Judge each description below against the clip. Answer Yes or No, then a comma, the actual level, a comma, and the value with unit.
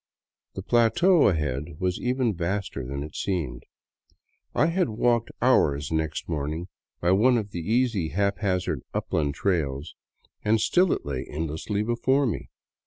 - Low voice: Yes, very low, 95 Hz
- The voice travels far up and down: Yes, wide, 7.2 semitones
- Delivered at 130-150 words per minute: Yes, average, 140 wpm